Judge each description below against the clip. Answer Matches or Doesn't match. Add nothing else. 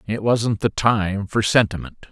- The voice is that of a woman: Doesn't match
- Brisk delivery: Doesn't match